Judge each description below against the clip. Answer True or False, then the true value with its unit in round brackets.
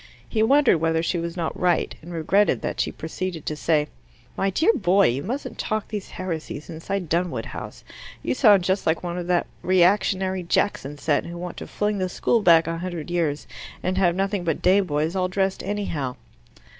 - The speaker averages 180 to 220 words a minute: True (195 wpm)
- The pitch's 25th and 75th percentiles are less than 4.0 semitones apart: True (3.0 semitones)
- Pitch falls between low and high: True (180 Hz)